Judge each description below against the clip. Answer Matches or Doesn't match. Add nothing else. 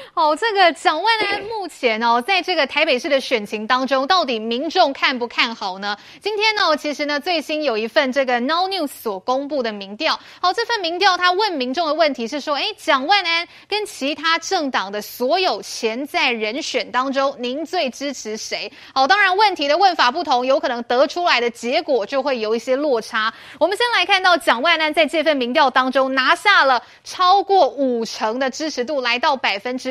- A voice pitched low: Doesn't match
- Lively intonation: Matches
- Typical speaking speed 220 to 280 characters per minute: Doesn't match